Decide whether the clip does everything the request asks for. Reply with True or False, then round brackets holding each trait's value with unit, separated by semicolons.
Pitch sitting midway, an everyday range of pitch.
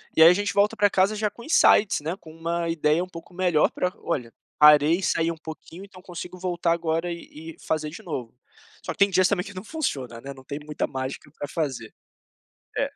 True (170 Hz; 3.6 semitones)